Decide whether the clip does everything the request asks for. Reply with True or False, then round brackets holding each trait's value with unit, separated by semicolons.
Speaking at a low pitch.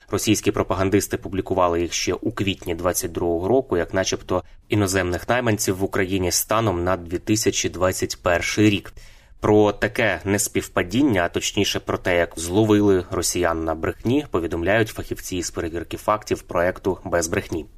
True (95 Hz)